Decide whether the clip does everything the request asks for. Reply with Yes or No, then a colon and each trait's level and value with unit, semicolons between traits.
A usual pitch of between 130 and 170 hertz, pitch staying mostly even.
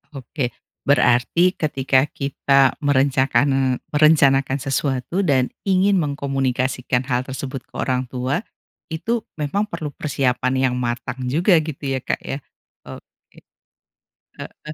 Yes: low, 135 Hz; narrow, 2.3 semitones